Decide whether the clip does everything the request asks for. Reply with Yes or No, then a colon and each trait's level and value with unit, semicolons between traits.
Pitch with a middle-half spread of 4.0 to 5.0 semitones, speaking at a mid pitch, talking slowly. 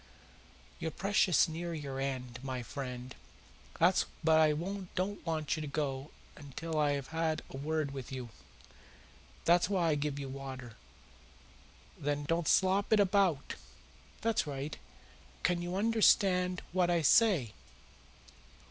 Yes: average, 4.7 semitones; medium, 155 Hz; slow, 130 wpm